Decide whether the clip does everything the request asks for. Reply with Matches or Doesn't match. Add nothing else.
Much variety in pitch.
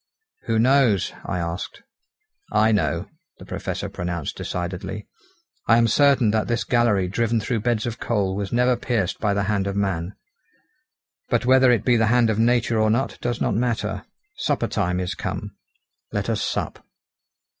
Doesn't match